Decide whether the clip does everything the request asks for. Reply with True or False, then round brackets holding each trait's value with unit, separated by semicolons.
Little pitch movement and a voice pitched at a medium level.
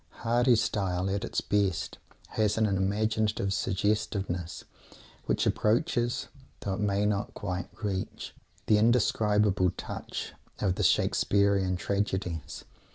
False (2.1 semitones; 100 Hz)